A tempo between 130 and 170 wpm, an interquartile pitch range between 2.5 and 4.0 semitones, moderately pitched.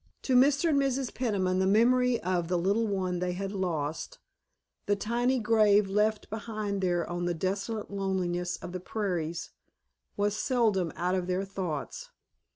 No: average, 160 wpm; average, 3.7 semitones; high, 195 Hz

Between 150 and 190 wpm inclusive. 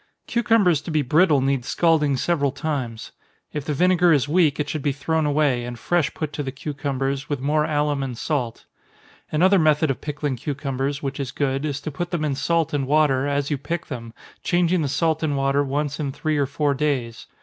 No: fast, 205 wpm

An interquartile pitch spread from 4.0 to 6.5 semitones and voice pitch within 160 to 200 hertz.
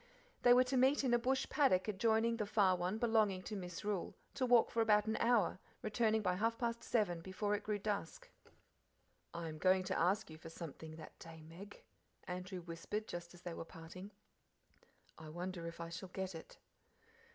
Yes: average, 4.4 semitones; high, 190 Hz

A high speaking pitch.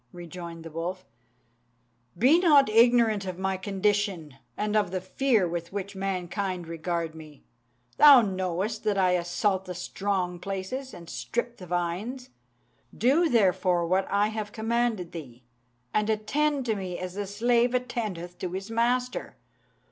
Yes: high, 195 Hz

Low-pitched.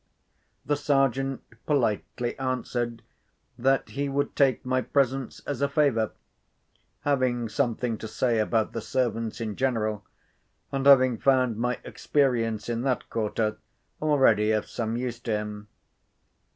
Yes: low, 125 Hz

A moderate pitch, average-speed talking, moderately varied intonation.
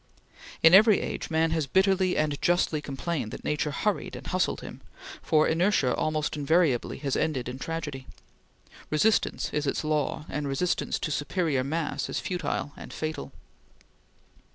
Yes: medium, 155 Hz; average, 150 wpm; average, 3.3 semitones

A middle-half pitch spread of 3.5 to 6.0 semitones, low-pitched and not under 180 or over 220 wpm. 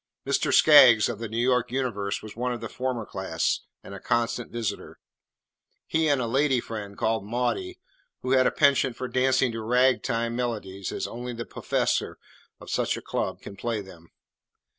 No: average, 2.9 semitones; low, 120 Hz; average, 185 wpm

